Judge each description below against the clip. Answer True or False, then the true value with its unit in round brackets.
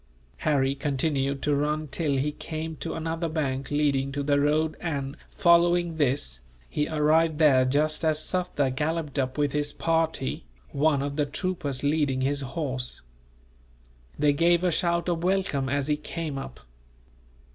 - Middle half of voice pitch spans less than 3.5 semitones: True (2.7 semitones)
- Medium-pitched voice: True (150 Hz)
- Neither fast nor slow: True (155 wpm)